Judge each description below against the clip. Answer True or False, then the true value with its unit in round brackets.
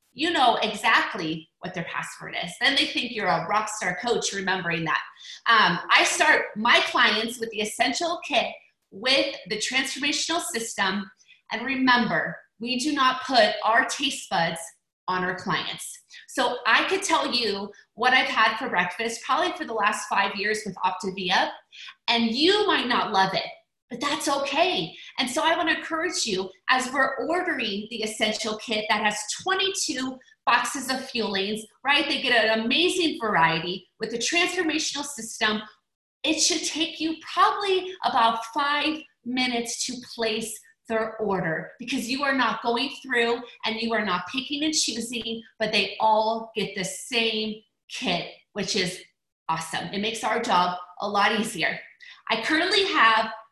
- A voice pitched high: True (235 Hz)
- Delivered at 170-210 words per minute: False (160 wpm)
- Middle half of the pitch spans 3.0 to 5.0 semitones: False (5.5 semitones)